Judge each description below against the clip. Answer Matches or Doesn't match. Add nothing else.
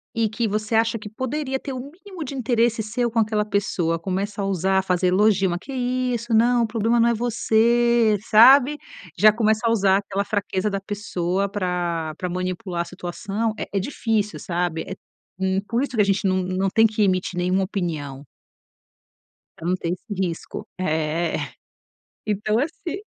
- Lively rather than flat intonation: Doesn't match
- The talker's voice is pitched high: Matches